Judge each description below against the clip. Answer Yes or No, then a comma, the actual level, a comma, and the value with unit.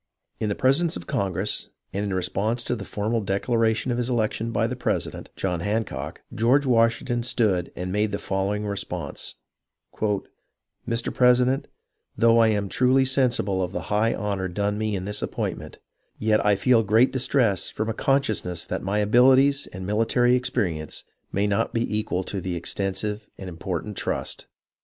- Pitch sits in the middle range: No, low, 105 Hz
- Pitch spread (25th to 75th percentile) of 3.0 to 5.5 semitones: Yes, average, 3.6 semitones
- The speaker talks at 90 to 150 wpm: No, average, 170 wpm